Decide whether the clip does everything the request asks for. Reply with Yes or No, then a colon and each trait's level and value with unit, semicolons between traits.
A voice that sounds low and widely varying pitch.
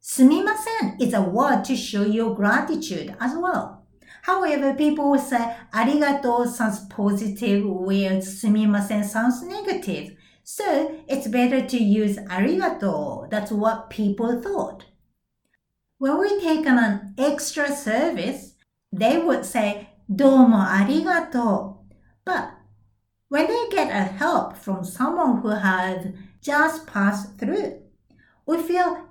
No: high, 240 Hz; wide, 6.2 semitones